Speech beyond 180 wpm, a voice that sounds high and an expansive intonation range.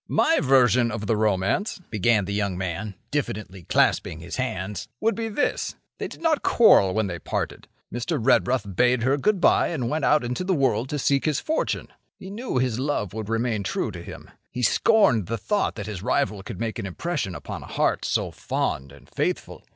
No: average, 200 wpm; low, 115 Hz; wide, 6.1 semitones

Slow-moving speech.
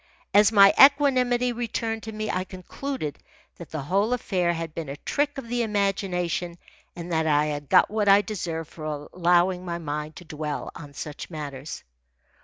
No: average, 175 wpm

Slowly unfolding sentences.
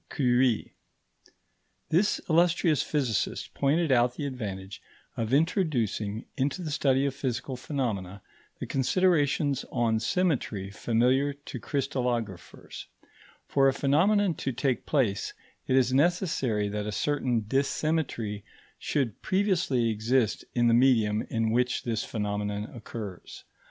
Yes: slow, 120 wpm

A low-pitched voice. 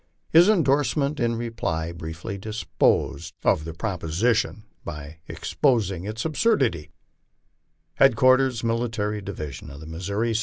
Yes: low, 110 Hz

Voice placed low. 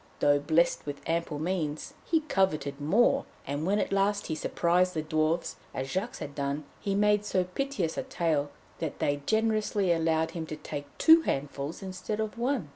No: medium, 170 Hz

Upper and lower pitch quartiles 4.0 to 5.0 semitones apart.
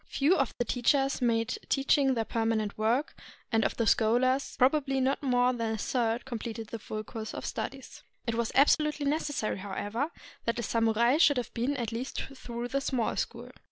No: average, 3.1 semitones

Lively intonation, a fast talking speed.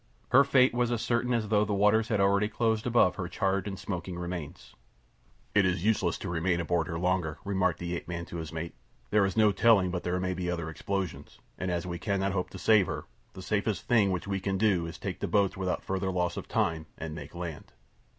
No: average, 3.1 semitones; fast, 240 wpm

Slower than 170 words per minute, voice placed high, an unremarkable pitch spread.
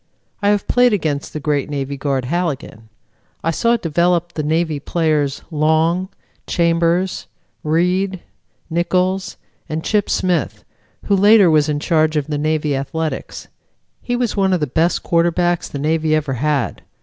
No: average, 150 wpm; medium, 165 Hz; average, 3.3 semitones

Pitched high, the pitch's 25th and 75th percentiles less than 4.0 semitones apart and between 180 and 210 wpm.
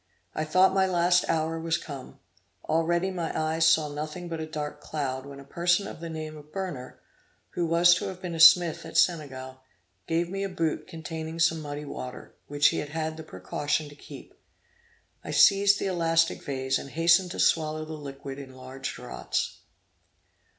No: medium, 160 Hz; average, 2.8 semitones; average, 185 wpm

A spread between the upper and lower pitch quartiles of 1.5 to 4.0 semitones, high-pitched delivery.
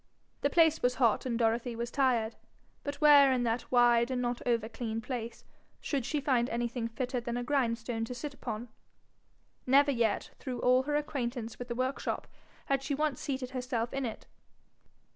Yes: narrow, 2.5 semitones; high, 245 Hz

